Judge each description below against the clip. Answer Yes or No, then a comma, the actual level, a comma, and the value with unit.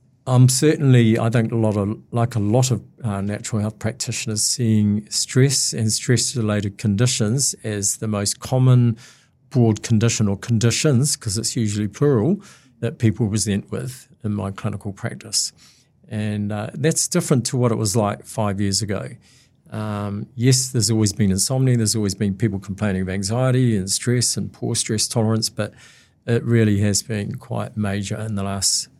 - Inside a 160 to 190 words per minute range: Yes, average, 170 wpm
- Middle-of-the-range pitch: No, low, 110 Hz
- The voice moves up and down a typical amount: Yes, average, 3.0 semitones